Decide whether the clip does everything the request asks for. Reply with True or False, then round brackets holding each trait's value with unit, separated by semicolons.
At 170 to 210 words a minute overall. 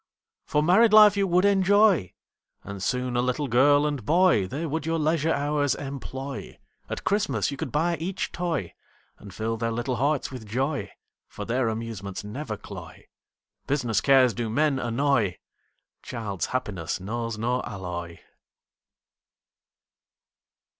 False (140 wpm)